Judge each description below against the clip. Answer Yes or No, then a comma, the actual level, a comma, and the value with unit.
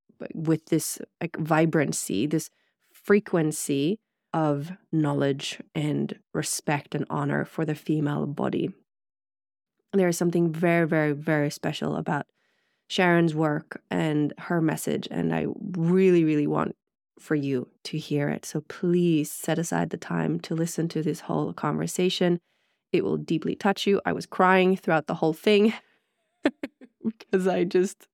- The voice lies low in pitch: No, medium, 165 Hz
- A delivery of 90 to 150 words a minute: Yes, average, 140 wpm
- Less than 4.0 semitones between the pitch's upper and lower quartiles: Yes, average, 3.3 semitones